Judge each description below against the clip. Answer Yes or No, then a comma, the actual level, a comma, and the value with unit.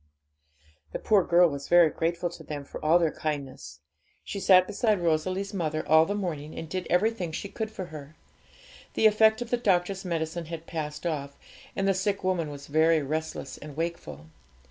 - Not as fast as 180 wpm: No, average, 185 wpm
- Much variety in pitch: No, average, 3.7 semitones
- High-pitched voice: No, medium, 170 Hz